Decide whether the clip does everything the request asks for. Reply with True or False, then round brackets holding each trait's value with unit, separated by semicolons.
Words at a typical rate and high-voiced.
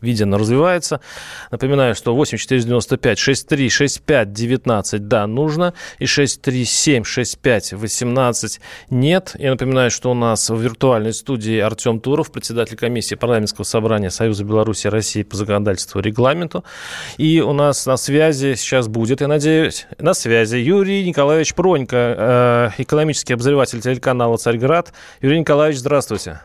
False (120 wpm; 125 Hz)